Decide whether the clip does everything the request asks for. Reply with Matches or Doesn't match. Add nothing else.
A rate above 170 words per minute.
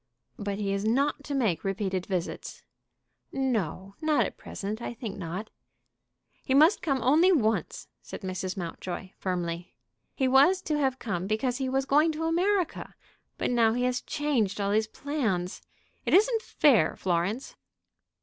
Doesn't match